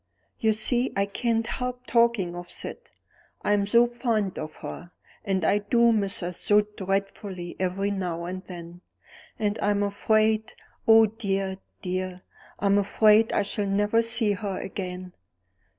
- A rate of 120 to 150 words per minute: Yes, average, 145 wpm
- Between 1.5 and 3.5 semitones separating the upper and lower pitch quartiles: Yes, average, 2.9 semitones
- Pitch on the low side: No, high, 200 Hz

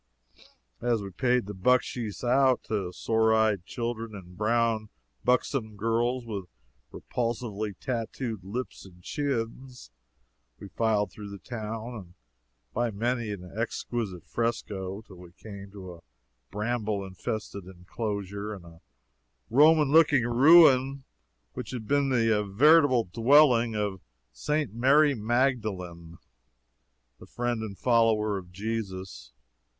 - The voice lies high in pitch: No, low, 110 Hz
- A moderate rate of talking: No, slow, 120 wpm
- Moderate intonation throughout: Yes, average, 3.5 semitones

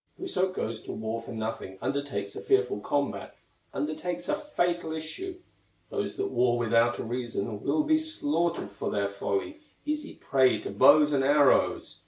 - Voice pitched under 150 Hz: Yes, medium, 140 Hz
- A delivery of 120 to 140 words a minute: No, average, 160 wpm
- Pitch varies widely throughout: Yes, wide, 8.2 semitones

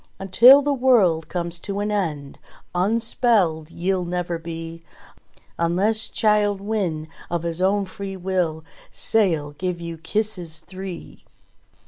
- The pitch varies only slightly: No, average, 3.7 semitones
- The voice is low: No, medium, 185 Hz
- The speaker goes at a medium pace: No, slow, 120 wpm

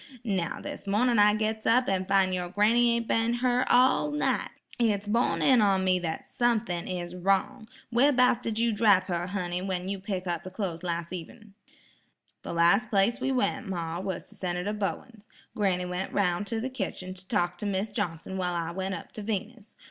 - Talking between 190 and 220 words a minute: Yes, average, 200 wpm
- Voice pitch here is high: Yes, high, 200 Hz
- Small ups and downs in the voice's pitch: No, average, 4.0 semitones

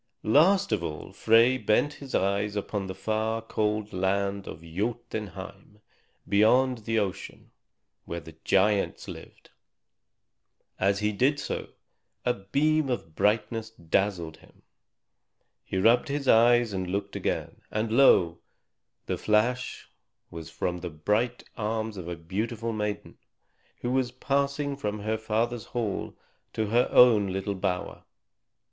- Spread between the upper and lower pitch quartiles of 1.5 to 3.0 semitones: No, average, 3.7 semitones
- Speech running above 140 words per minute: No, slow, 135 wpm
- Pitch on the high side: No, low, 105 Hz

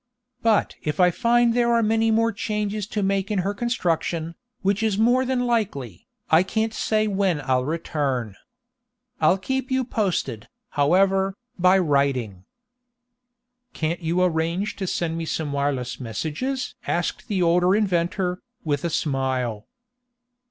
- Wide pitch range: Yes, wide, 6.1 semitones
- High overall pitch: No, medium, 180 Hz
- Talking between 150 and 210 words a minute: No, average, 140 wpm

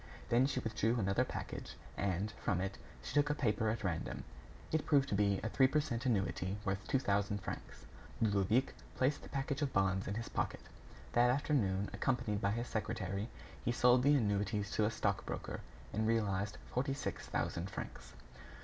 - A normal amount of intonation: Yes, average, 4.3 semitones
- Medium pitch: No, low, 110 Hz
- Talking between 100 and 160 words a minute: No, average, 180 wpm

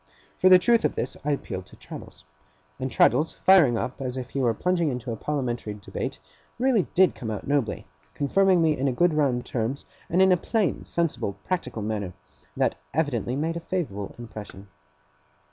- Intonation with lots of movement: Yes, wide, 6.8 semitones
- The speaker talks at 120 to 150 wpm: No, average, 180 wpm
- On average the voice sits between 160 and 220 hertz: No, medium, 140 Hz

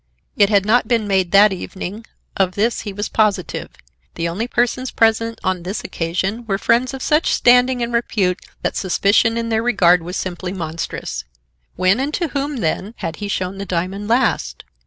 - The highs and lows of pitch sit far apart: No, average, 4.1 semitones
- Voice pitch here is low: No, high, 205 Hz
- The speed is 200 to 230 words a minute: No, average, 180 wpm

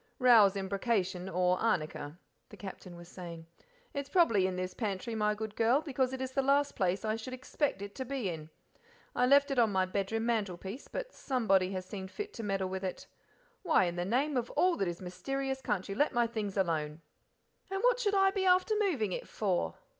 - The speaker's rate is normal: No, fast, 215 wpm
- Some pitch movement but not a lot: No, wide, 6.1 semitones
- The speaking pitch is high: Yes, high, 215 Hz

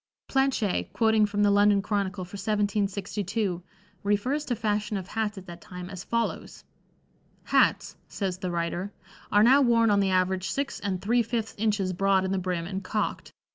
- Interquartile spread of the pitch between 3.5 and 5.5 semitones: No, narrow, 2.6 semitones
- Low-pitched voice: No, high, 200 Hz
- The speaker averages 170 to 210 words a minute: Yes, average, 175 wpm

